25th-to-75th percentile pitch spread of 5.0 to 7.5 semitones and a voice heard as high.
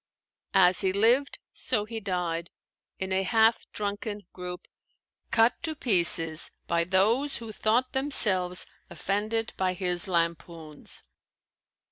No: average, 4.0 semitones; high, 195 Hz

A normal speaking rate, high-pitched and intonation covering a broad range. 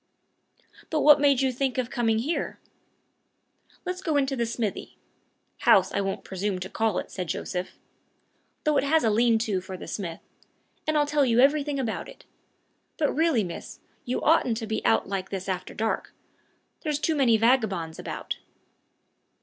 Yes: average, 170 wpm; high, 235 Hz; wide, 6.5 semitones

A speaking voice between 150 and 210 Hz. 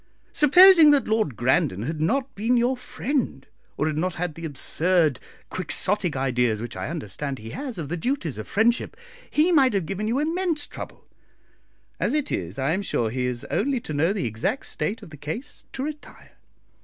Yes: medium, 185 Hz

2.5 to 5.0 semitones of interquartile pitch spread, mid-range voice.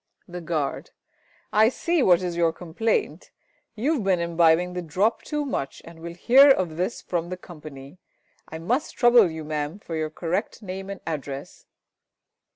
Yes: average, 4.6 semitones; medium, 175 Hz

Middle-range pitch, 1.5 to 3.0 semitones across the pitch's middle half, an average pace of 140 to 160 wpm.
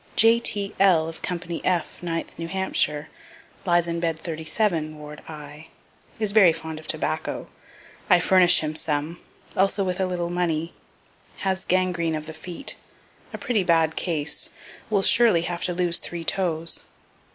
Yes: medium, 170 Hz; narrow, 2.6 semitones; average, 150 wpm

